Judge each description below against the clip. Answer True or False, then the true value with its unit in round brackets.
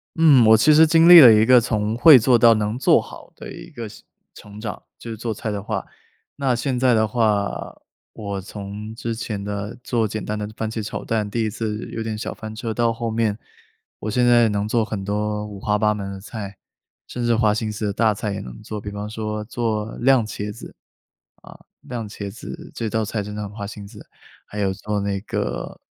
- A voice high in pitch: False (110 Hz)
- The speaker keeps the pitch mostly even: True (2.0 semitones)